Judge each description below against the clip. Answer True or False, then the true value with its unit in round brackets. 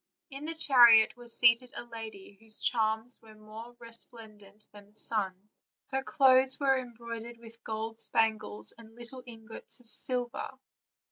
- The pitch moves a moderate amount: False (2.1 semitones)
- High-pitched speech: True (230 Hz)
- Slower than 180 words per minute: True (150 wpm)